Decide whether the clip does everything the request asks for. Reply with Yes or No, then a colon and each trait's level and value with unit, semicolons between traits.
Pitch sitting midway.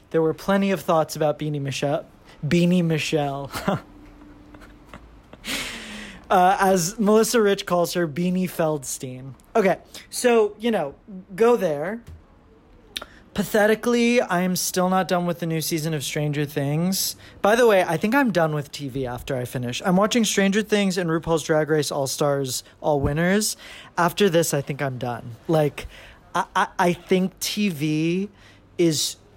Yes: medium, 170 Hz